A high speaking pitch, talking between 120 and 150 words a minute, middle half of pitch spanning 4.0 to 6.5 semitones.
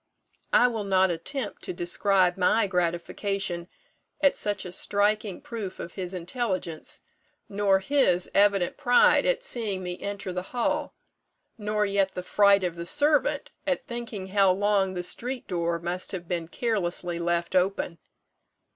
No: high, 195 Hz; average, 145 wpm; average, 3.0 semitones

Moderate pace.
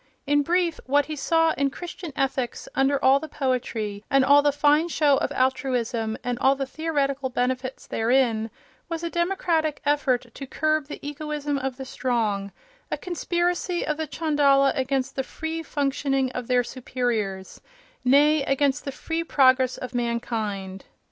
Yes: average, 155 wpm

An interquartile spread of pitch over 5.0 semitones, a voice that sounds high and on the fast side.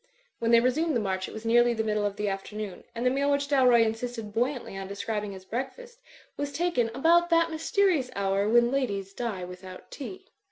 Yes: wide, 5.5 semitones; high, 235 Hz; fast, 210 wpm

